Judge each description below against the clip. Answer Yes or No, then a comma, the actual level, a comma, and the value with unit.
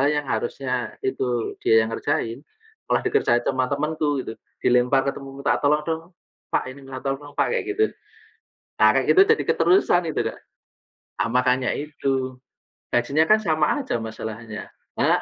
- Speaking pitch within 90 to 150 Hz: Yes, low, 135 Hz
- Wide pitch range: No, average, 3.3 semitones